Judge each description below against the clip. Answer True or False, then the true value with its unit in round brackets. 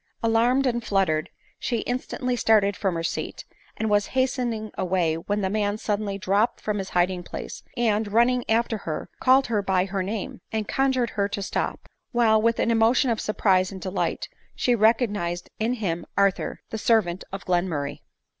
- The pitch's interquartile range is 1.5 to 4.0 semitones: True (3.6 semitones)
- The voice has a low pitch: False (210 Hz)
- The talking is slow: False (175 wpm)